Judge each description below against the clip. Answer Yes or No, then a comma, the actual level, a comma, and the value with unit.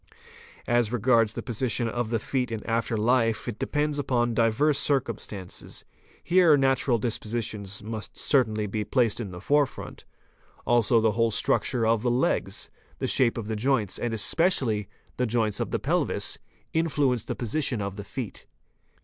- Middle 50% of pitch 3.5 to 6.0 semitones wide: No, average, 3.1 semitones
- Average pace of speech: Yes, average, 160 wpm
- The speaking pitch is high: No, low, 115 Hz